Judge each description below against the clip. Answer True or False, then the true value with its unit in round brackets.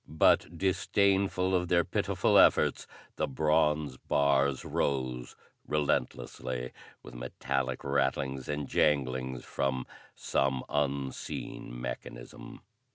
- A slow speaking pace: True (95 wpm)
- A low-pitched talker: True (70 Hz)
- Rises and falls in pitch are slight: False (3.0 semitones)